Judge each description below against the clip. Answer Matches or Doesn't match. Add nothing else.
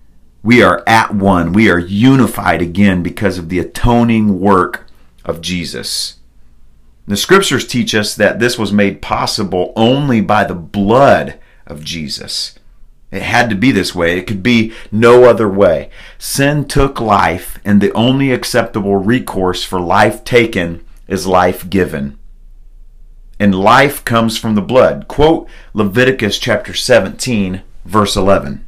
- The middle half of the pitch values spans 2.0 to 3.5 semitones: Doesn't match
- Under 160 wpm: Matches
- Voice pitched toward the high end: Doesn't match